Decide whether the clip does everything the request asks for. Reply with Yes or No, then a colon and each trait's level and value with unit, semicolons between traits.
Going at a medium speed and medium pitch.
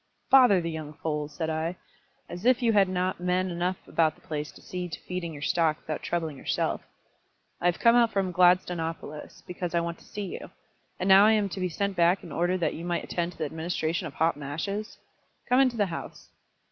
No: fast, 220 wpm; medium, 175 Hz